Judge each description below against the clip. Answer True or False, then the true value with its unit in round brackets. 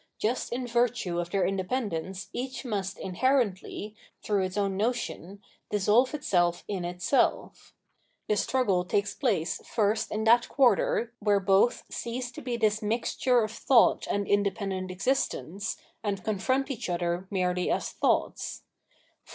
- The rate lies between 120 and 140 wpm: True (135 wpm)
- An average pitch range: True (4.2 semitones)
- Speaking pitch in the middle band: False (205 Hz)